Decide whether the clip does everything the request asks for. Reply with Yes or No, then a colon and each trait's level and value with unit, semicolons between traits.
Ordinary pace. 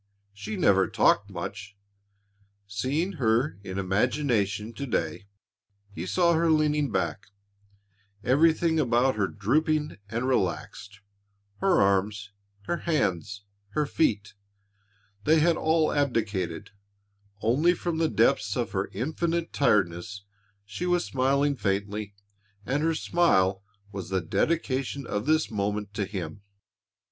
No: slow, 120 wpm